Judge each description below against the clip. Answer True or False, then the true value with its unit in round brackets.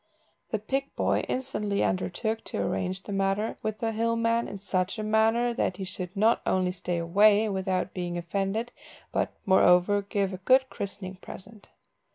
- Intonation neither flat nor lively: True (3.0 semitones)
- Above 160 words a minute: True (170 wpm)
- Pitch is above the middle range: True (200 Hz)